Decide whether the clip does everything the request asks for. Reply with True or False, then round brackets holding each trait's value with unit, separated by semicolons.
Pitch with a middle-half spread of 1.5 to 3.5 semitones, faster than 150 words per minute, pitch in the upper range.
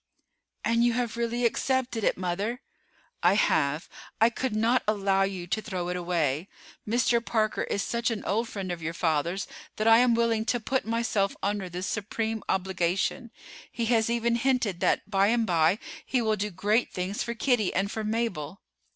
False (3.9 semitones; 180 wpm; 215 Hz)